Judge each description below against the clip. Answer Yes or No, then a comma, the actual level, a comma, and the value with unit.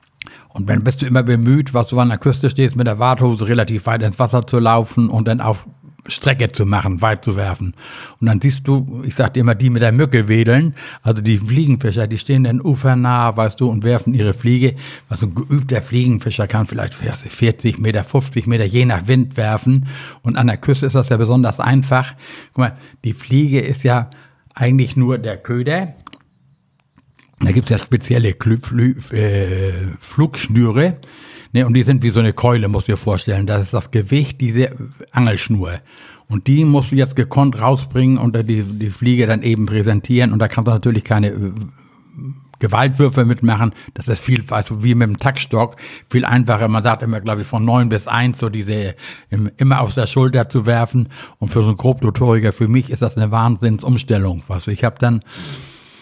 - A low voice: Yes, low, 120 Hz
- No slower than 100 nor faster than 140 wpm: No, average, 185 wpm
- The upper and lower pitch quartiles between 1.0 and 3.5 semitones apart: Yes, average, 2.7 semitones